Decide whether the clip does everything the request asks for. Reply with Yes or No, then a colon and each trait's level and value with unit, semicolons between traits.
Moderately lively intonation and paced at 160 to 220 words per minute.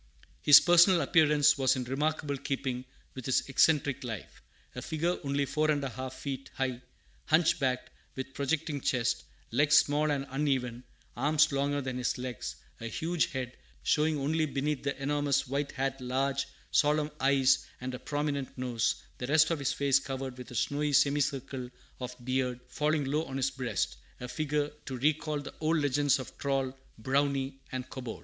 No: narrow, 2.3 semitones; average, 170 wpm